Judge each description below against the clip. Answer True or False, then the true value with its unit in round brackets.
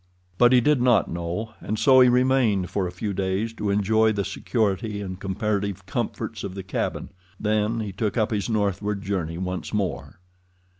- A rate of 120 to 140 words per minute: False (180 wpm)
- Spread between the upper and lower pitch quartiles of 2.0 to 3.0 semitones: True (2.7 semitones)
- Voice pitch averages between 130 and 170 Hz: False (105 Hz)